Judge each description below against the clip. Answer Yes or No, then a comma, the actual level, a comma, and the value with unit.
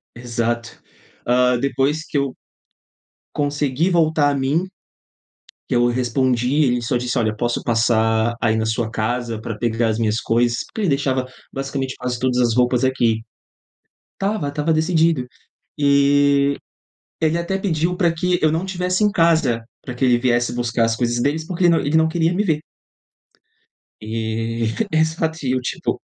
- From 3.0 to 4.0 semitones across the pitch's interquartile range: No, average, 5.0 semitones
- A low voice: Yes, low, 130 Hz